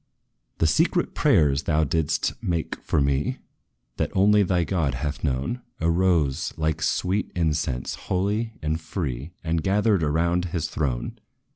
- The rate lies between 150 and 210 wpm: No, slow, 135 wpm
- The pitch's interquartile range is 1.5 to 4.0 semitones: Yes, average, 3.7 semitones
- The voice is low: Yes, very low, 80 Hz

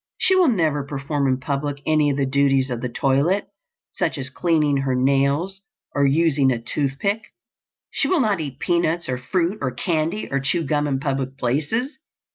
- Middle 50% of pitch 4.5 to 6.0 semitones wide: No, average, 3.8 semitones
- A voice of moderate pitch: Yes, medium, 145 Hz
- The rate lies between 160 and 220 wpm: Yes, average, 185 wpm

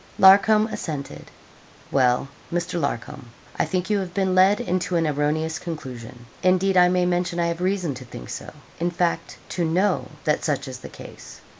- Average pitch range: Yes, average, 3.4 semitones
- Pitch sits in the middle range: Yes, medium, 175 Hz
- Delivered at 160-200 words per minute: Yes, average, 175 wpm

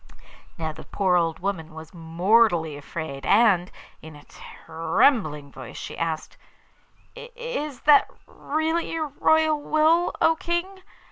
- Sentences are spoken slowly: Yes, slow, 125 wpm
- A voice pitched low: No, high, 195 Hz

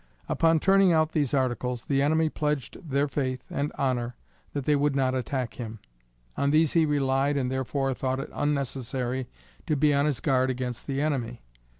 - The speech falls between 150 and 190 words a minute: Yes, average, 180 wpm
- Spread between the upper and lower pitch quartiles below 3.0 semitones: Yes, narrow, 2.4 semitones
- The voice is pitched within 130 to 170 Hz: Yes, low, 135 Hz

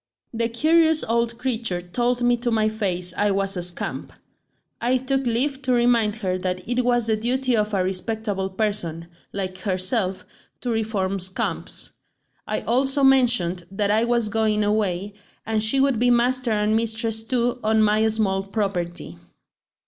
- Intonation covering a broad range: No, average, 3.7 semitones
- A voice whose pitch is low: No, high, 220 Hz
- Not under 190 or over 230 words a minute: No, average, 160 wpm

